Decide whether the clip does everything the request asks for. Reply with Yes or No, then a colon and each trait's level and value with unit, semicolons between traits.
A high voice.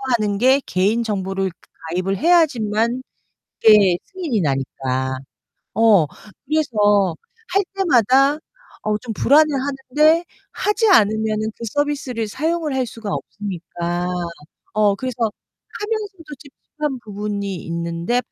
Yes: high, 225 Hz